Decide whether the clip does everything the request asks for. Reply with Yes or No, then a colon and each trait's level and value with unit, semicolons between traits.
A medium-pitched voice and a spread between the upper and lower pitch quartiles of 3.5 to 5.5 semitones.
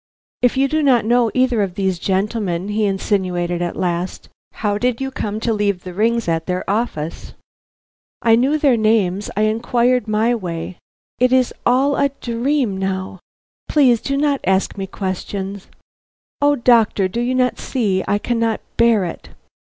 No: high, 215 Hz; average, 4.4 semitones